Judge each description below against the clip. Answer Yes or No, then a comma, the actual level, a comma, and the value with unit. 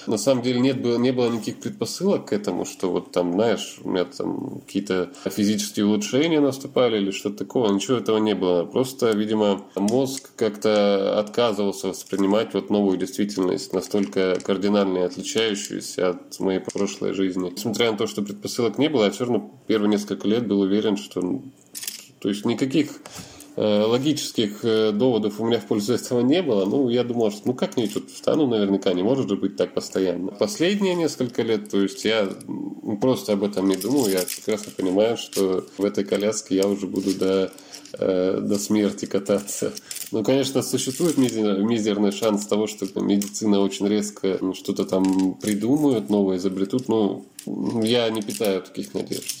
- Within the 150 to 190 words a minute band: Yes, fast, 160 wpm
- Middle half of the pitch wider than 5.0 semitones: No, average, 2.8 semitones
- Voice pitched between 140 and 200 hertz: No, low, 105 Hz